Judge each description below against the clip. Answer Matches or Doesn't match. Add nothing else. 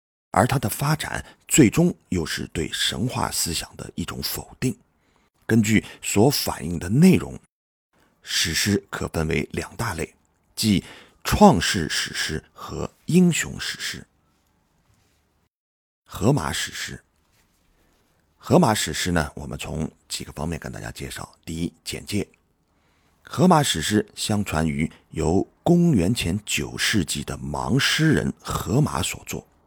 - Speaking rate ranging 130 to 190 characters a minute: Matches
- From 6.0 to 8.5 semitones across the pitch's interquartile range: Doesn't match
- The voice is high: Doesn't match